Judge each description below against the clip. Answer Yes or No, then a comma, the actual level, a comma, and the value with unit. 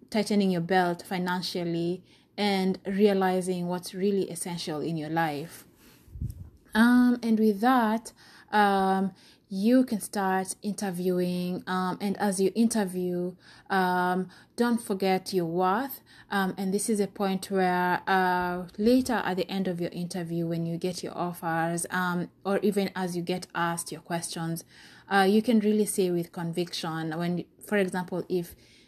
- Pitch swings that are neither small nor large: No, narrow, 2.3 semitones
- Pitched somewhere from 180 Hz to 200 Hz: Yes, medium, 185 Hz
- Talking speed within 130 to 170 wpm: Yes, average, 150 wpm